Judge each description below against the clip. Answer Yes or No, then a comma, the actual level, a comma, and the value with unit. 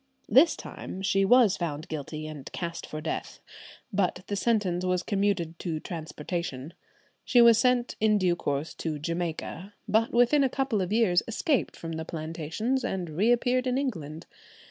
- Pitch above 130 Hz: Yes, medium, 185 Hz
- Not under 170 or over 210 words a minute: No, average, 160 wpm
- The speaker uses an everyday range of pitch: No, wide, 6.1 semitones